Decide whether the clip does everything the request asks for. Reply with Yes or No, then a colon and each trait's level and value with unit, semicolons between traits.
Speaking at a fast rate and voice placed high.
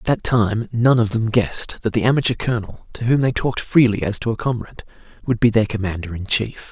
No: fast, 230 wpm; low, 115 Hz